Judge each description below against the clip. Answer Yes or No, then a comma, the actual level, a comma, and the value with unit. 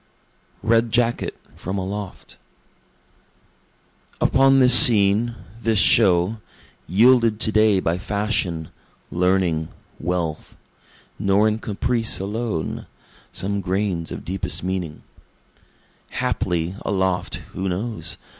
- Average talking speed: No, slow, 95 wpm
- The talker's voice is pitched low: Yes, low, 100 Hz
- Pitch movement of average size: Yes, average, 3.8 semitones